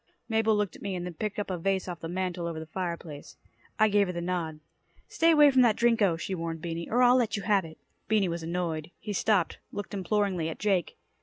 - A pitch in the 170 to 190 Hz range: Yes, medium, 185 Hz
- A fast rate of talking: Yes, fast, 240 wpm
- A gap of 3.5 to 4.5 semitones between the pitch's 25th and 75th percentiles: Yes, average, 3.9 semitones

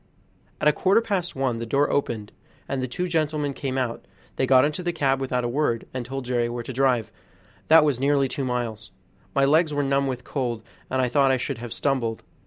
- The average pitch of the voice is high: No, low, 135 Hz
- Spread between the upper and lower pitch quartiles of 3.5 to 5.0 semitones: No, average, 3.0 semitones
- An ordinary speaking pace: No, fast, 220 wpm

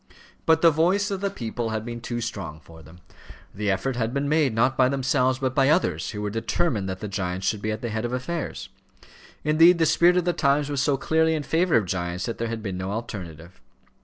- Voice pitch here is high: No, low, 120 Hz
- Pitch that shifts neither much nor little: No, wide, 7.1 semitones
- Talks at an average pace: No, fast, 235 wpm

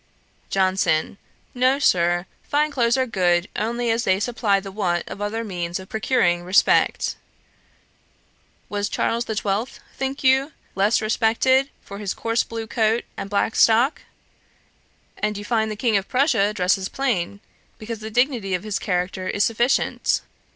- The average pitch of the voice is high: Yes, high, 215 Hz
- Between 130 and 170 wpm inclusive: Yes, average, 150 wpm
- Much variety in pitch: No, average, 3.7 semitones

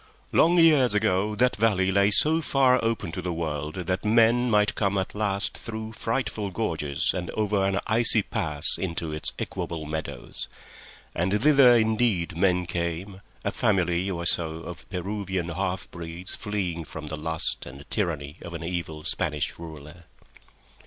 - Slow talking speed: No, average, 155 wpm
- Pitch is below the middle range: Yes, very low, 95 Hz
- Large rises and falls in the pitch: No, average, 4.4 semitones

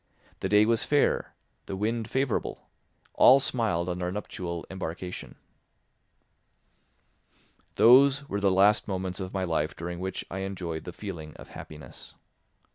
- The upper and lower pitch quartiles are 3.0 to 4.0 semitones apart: Yes, average, 3.6 semitones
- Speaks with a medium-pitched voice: No, very low, 95 Hz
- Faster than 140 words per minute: No, slow, 135 wpm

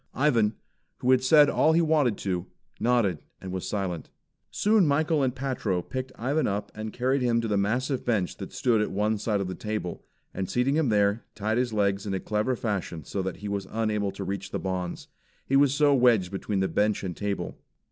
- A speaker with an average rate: No, fast, 210 wpm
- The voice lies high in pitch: No, low, 110 Hz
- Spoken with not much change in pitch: No, average, 4.7 semitones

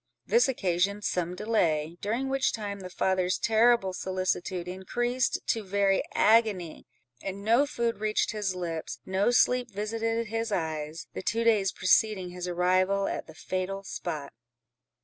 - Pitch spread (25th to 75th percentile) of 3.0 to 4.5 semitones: Yes, average, 3.8 semitones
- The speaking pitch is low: No, high, 195 Hz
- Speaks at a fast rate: No, average, 145 wpm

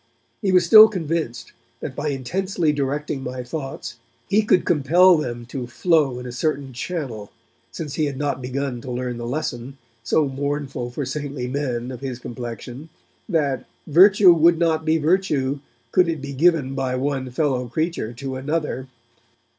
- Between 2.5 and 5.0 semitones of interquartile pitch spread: Yes, average, 4.1 semitones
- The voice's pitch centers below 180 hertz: Yes, medium, 140 Hz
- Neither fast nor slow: Yes, average, 160 wpm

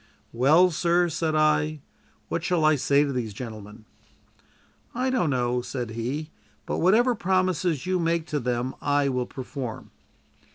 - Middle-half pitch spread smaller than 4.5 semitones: No, wide, 5.5 semitones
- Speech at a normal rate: Yes, average, 150 wpm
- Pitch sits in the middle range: Yes, medium, 150 Hz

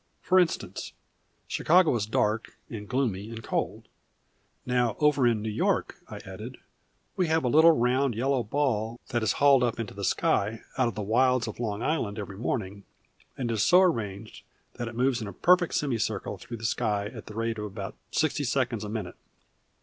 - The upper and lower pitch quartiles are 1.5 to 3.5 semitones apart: No, average, 4.0 semitones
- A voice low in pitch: Yes, low, 115 Hz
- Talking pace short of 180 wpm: No, average, 190 wpm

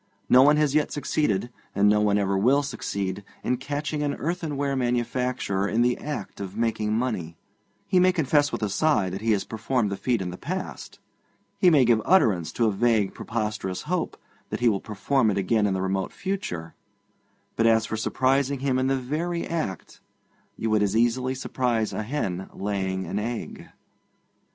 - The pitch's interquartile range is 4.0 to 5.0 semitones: No, wide, 5.4 semitones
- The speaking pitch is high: No, low, 115 Hz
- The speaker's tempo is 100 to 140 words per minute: No, average, 185 wpm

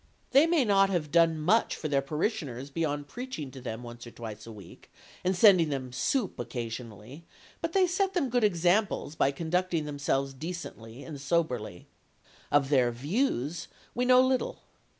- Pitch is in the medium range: Yes, medium, 155 Hz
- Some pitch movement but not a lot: No, wide, 7.4 semitones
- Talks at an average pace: Yes, average, 165 wpm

